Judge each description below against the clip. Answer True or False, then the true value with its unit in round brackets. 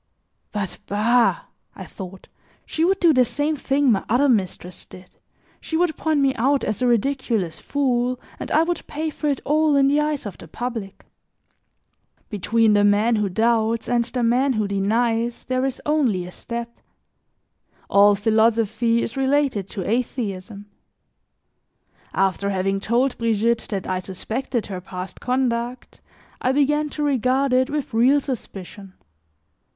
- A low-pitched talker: False (235 Hz)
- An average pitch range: True (4.8 semitones)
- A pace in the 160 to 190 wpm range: False (150 wpm)